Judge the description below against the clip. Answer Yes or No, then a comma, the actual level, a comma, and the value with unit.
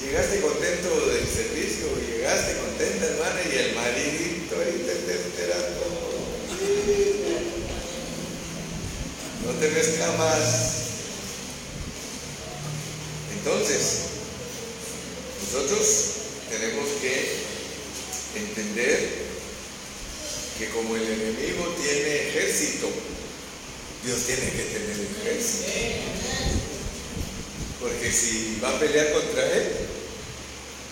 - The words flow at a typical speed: No, slow, 75 wpm